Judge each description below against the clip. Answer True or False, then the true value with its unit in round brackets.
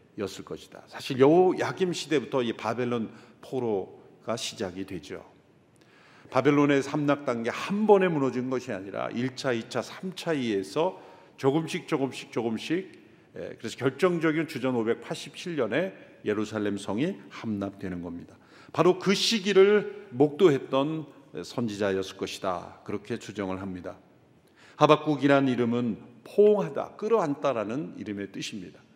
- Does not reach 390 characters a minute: True (285 characters per minute)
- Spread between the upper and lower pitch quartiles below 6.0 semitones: False (6.6 semitones)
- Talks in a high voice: False (135 Hz)